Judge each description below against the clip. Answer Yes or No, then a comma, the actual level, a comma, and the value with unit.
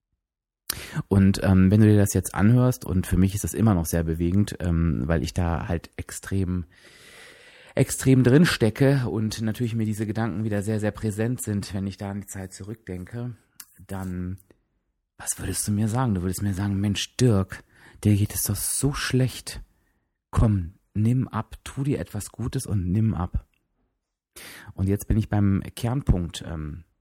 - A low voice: Yes, low, 100 Hz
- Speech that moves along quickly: No, average, 175 wpm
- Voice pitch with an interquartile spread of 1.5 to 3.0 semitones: No, average, 3.4 semitones